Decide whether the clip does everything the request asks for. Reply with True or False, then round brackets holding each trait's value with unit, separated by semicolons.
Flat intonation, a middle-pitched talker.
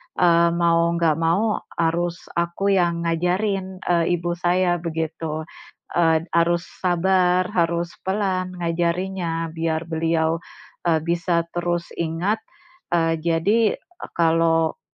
True (1.4 semitones; 170 Hz)